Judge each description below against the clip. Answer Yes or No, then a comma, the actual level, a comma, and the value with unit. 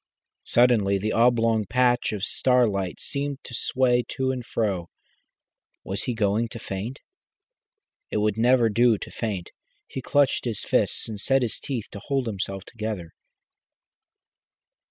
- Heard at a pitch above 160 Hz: No, low, 115 Hz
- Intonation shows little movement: No, average, 3.4 semitones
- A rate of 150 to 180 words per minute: No, average, 140 wpm